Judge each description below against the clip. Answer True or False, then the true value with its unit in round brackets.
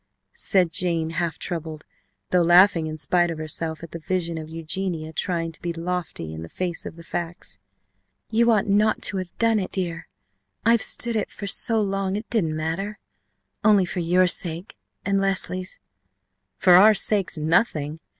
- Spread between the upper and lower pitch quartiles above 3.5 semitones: False (3.1 semitones)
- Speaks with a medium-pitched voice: True (175 Hz)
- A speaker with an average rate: True (175 wpm)